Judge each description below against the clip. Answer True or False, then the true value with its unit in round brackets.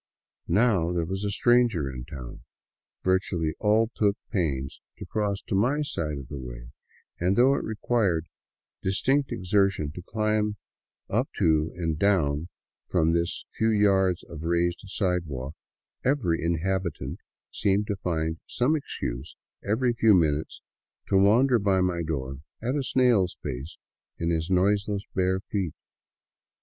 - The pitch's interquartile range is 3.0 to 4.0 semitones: False (4.6 semitones)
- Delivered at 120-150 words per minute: True (140 wpm)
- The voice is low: True (95 Hz)